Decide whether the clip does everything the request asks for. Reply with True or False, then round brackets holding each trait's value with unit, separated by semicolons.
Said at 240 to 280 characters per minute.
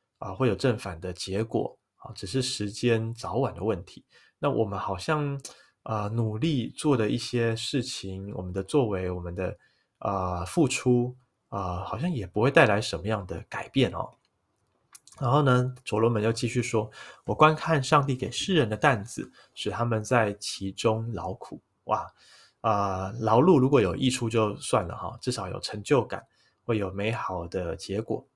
True (250 characters per minute)